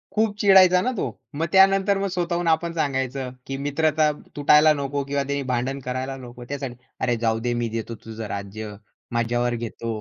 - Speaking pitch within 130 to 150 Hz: Yes, low, 135 Hz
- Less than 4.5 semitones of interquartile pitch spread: No, average, 5.3 semitones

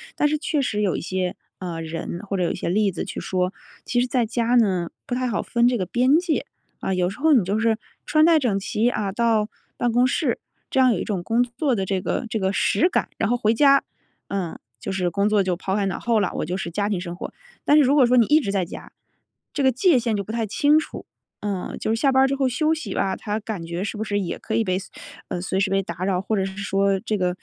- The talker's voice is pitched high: Yes, high, 210 Hz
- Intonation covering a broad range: No, average, 4.6 semitones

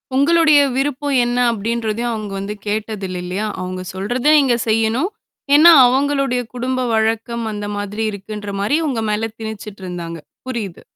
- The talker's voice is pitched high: Yes, high, 225 Hz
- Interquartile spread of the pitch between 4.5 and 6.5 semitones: No, average, 3.8 semitones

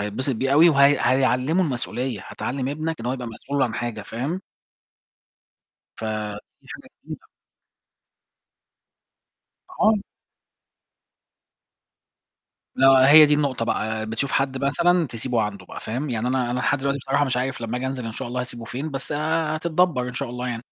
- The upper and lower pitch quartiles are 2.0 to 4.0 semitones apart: Yes, average, 3.1 semitones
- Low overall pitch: Yes, low, 130 Hz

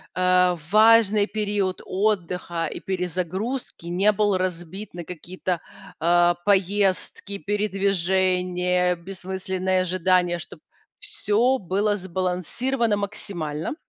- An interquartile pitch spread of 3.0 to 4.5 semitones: No, narrow, 2.4 semitones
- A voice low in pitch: No, medium, 185 Hz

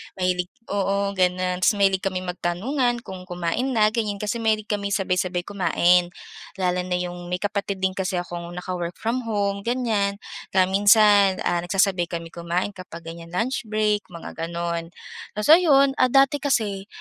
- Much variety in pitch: No, average, 3.0 semitones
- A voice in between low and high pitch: No, high, 195 Hz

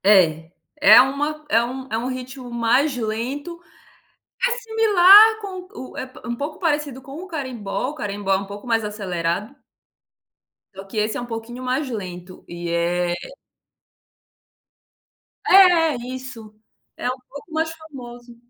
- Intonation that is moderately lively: No, wide, 6.4 semitones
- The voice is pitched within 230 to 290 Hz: Yes, very high, 250 Hz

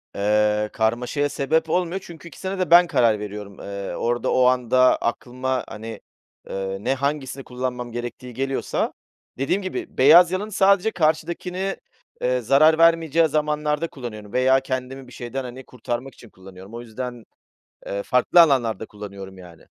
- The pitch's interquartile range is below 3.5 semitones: No, wide, 5.5 semitones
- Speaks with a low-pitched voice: Yes, low, 130 Hz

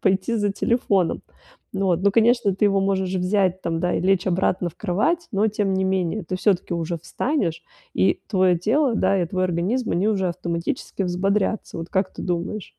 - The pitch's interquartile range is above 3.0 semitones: No, narrow, 2.6 semitones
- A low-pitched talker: No, high, 190 Hz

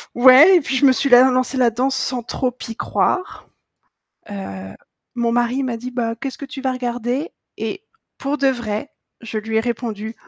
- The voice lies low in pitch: No, high, 245 Hz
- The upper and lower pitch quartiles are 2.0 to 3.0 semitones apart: Yes, narrow, 2.5 semitones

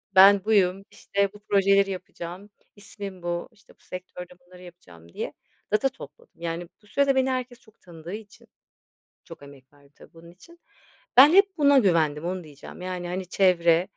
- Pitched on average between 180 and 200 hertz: Yes, medium, 185 Hz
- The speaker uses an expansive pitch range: No, average, 3.4 semitones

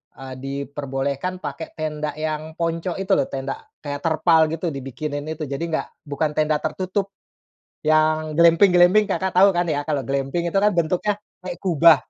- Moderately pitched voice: Yes, medium, 155 Hz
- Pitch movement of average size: Yes, average, 3.3 semitones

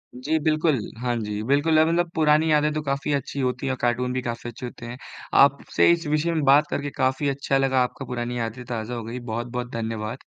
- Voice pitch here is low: Yes, low, 130 Hz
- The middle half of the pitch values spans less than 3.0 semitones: No, average, 3.7 semitones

